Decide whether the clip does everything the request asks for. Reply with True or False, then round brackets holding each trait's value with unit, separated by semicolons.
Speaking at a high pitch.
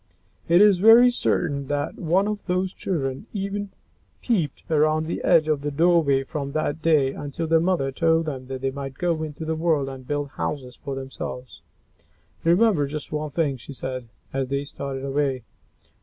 False (150 Hz)